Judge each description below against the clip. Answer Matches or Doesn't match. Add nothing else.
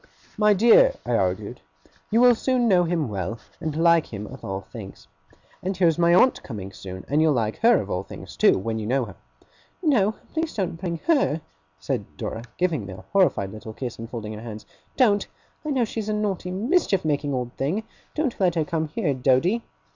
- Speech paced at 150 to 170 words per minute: Doesn't match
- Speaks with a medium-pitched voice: Matches